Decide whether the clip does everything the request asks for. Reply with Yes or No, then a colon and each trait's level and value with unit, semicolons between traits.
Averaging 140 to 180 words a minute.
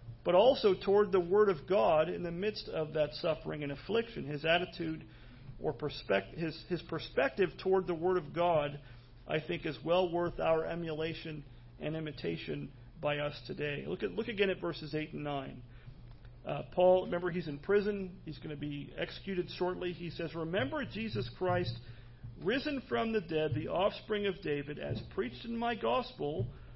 Yes: average, 175 wpm